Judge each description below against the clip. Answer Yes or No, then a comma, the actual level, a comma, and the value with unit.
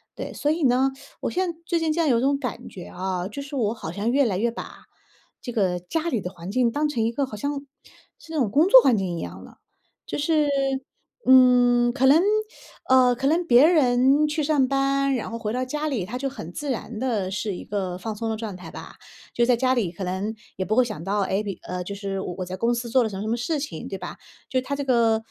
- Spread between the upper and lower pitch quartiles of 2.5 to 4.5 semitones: No, average, 5.3 semitones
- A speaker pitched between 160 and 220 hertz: No, high, 240 Hz